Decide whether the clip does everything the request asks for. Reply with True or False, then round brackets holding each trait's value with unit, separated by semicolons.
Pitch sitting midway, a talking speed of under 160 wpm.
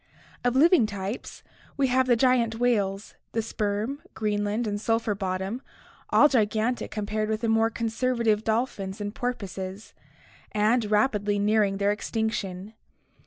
False (220 Hz; 135 wpm)